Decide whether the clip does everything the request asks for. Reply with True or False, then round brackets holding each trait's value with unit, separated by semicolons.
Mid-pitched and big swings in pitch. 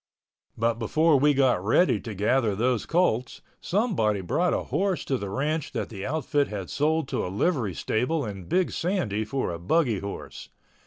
False (125 Hz; 7.1 semitones)